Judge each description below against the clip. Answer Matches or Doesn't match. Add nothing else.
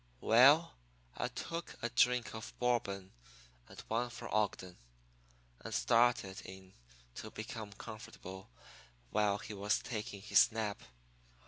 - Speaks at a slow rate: Matches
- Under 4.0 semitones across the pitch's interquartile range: Matches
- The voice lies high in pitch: Doesn't match